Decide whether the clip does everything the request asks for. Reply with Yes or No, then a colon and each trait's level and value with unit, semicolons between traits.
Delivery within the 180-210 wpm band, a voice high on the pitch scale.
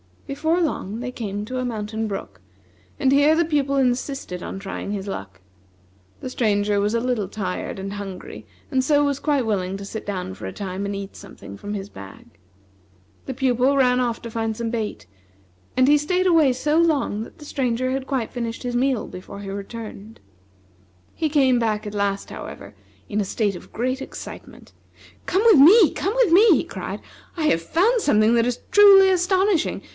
Yes: average, 190 wpm; high, 240 Hz